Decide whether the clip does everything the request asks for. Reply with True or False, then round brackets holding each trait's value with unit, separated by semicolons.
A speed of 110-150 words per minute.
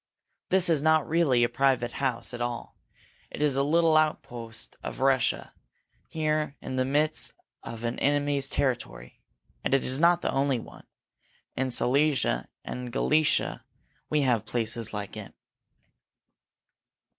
True (145 wpm)